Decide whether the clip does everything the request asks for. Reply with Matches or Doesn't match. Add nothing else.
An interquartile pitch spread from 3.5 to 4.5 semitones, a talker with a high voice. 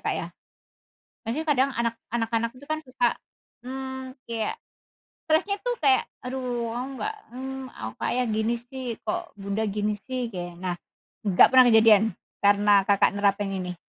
Matches